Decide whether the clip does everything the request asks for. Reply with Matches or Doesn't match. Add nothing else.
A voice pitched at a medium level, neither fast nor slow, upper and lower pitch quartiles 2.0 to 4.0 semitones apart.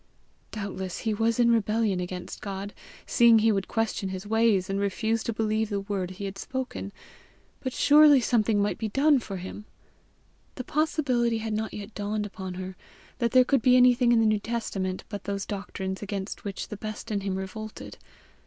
Doesn't match